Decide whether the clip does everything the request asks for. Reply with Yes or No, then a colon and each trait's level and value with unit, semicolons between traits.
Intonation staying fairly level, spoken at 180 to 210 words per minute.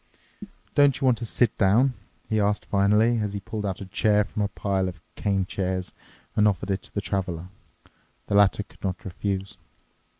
Yes: narrow, 1.8 semitones; average, 190 wpm